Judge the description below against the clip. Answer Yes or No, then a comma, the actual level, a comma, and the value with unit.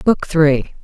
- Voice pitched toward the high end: No, medium, 155 Hz